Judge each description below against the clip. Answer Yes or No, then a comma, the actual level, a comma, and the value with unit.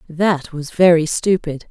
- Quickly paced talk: No, average, 140 wpm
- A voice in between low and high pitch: Yes, medium, 165 Hz